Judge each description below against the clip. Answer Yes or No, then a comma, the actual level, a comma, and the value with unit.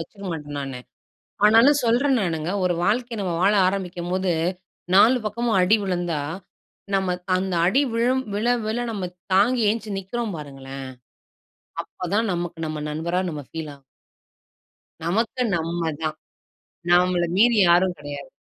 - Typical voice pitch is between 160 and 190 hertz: Yes, medium, 185 Hz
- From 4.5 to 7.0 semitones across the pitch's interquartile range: Yes, average, 5.0 semitones